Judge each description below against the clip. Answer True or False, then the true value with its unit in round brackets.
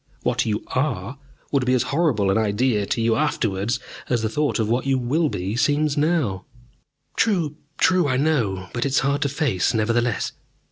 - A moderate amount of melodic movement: True (4.9 semitones)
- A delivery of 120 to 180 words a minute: False (190 wpm)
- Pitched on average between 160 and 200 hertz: False (125 Hz)